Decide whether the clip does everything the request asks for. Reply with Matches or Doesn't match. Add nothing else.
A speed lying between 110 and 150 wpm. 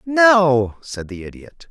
Matches